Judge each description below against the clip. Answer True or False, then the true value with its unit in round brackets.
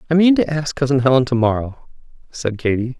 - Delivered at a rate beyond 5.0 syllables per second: True (5.9 syllables/s)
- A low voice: True (130 Hz)